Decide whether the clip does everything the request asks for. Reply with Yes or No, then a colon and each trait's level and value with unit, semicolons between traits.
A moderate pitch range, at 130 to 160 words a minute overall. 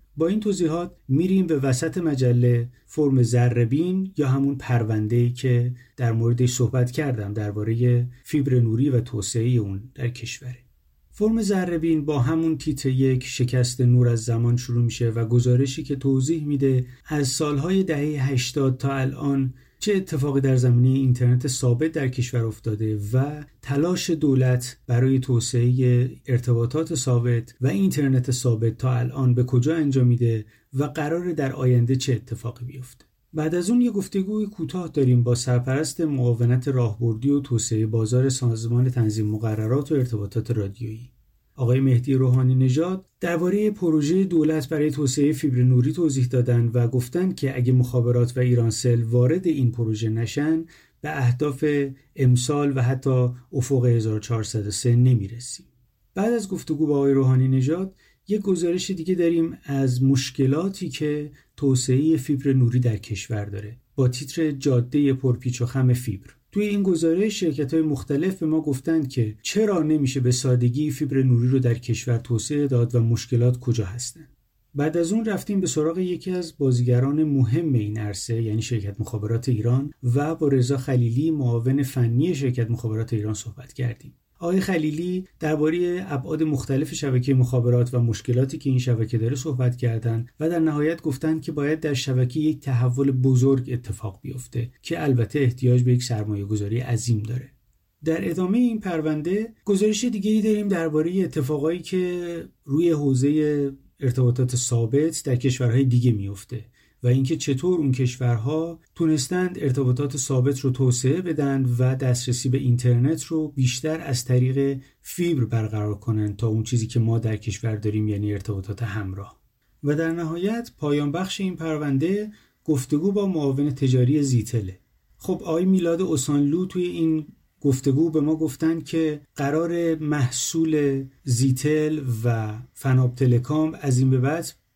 Yes: average, 4.3 semitones; average, 150 wpm